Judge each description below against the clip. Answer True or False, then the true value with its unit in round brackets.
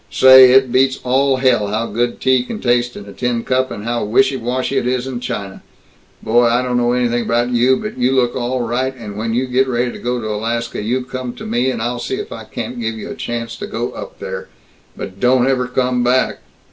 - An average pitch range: False (1.6 semitones)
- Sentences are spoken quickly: True (235 wpm)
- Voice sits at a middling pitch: False (125 Hz)